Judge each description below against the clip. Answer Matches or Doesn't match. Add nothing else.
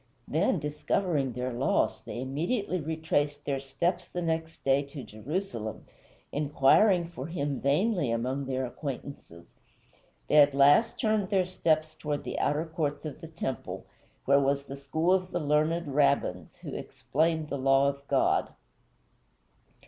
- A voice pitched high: Doesn't match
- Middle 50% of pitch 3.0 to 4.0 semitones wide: Matches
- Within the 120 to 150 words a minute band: Matches